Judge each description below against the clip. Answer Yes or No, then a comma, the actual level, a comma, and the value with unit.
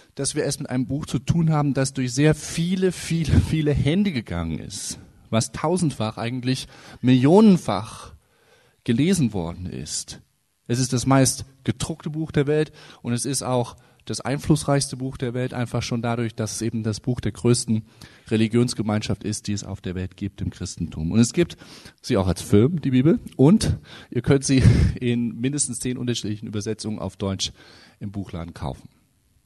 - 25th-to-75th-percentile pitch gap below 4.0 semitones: No, average, 4.8 semitones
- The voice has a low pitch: Yes, low, 120 Hz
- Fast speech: No, average, 175 wpm